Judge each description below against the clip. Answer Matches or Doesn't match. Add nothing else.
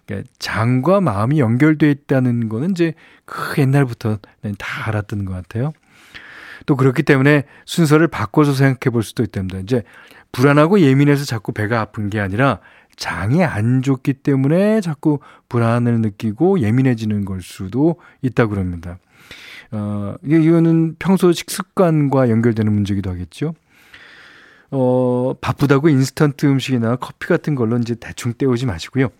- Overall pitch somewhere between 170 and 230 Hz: Doesn't match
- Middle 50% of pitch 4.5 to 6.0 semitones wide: Matches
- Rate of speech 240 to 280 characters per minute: Doesn't match